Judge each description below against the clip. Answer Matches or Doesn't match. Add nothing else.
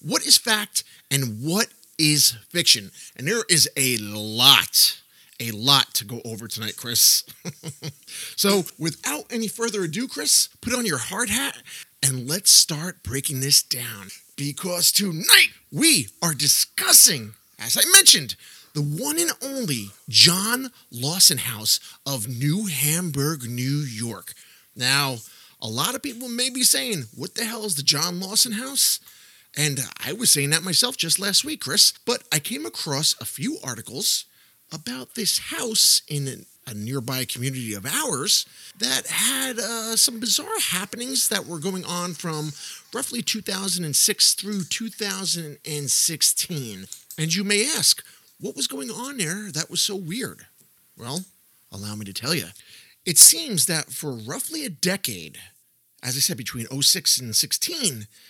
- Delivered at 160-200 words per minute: Doesn't match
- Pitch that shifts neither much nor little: Doesn't match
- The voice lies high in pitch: Doesn't match